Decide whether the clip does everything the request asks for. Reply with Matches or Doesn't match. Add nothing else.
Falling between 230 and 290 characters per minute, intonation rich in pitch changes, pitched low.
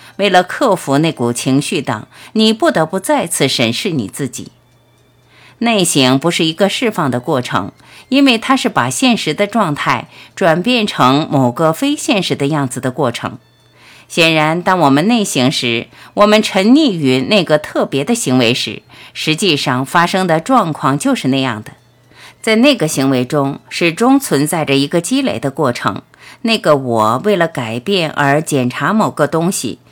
Doesn't match